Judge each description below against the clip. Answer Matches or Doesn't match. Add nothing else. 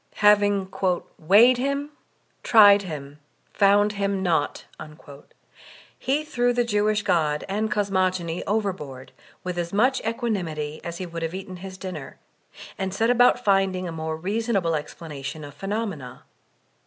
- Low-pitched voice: Doesn't match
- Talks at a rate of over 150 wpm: Doesn't match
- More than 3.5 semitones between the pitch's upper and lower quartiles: Matches